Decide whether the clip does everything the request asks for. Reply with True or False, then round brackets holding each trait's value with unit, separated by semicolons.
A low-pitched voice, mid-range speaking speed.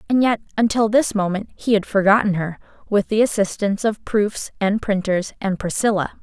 False (205 Hz; 175 wpm)